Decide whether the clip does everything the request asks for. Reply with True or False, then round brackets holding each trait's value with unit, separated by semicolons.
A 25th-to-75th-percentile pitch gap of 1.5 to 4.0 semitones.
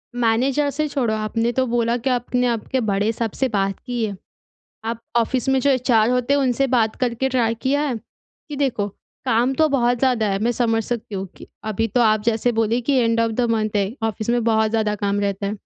True (2.5 semitones)